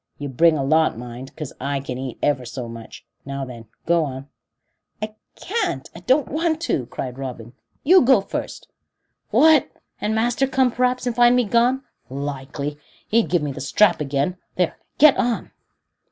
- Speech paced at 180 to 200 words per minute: No, average, 170 wpm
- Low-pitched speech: No, medium, 160 Hz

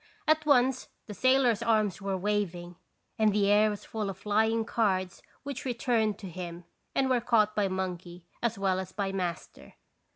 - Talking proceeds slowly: No, average, 170 wpm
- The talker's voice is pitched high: Yes, high, 210 Hz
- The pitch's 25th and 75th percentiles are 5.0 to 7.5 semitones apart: No, average, 3.7 semitones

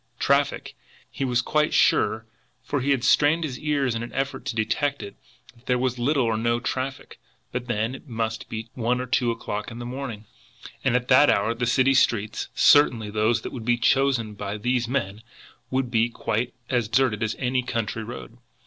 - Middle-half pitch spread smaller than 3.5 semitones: Yes, narrow, 2.6 semitones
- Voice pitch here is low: Yes, low, 120 Hz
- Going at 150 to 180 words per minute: No, average, 195 wpm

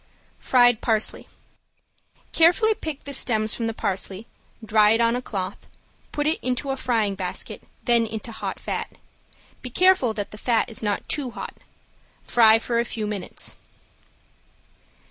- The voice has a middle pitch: No, high, 230 Hz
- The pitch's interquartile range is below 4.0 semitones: Yes, average, 2.8 semitones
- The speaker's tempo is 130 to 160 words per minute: Yes, average, 145 wpm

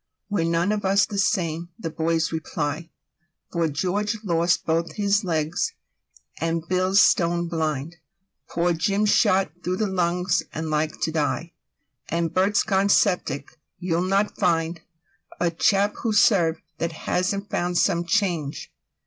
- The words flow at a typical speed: No, slow, 130 wpm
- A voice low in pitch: No, medium, 175 Hz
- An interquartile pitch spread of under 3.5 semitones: Yes, average, 3.0 semitones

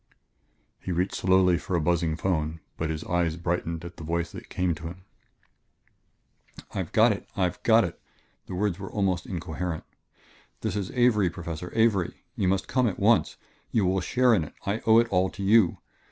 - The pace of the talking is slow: No, average, 185 wpm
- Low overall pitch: Yes, very low, 90 Hz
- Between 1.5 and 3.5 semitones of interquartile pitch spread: Yes, average, 2.9 semitones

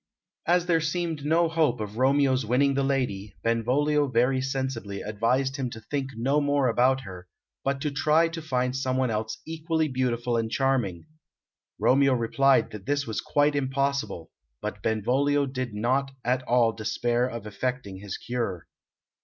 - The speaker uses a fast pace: No, average, 155 wpm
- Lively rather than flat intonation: No, average, 3.5 semitones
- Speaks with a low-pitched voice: Yes, low, 130 Hz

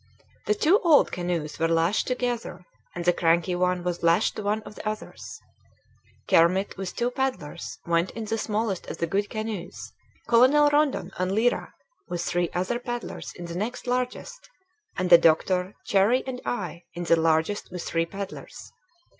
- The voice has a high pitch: Yes, high, 195 Hz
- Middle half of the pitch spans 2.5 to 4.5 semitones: No, wide, 5.6 semitones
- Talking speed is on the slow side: No, average, 170 wpm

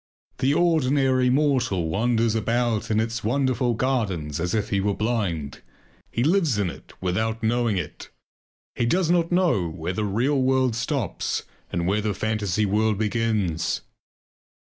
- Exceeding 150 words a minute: No, average, 145 wpm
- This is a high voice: No, low, 115 Hz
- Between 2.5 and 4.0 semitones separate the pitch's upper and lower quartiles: No, average, 4.4 semitones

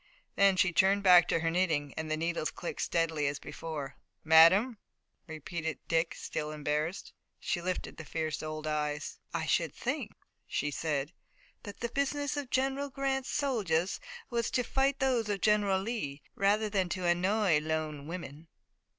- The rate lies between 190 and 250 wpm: No, average, 160 wpm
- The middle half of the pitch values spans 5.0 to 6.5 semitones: Yes, wide, 5.4 semitones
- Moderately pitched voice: Yes, medium, 175 Hz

